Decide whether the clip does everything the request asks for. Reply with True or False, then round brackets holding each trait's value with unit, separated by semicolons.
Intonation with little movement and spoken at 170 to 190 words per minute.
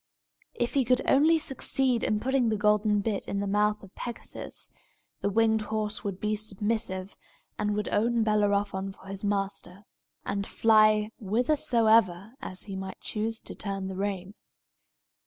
False (2.2 semitones; 150 wpm)